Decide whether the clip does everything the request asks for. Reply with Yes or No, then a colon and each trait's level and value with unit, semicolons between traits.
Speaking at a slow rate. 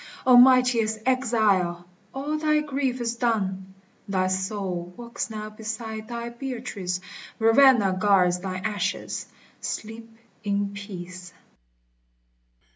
Yes: slow, 105 wpm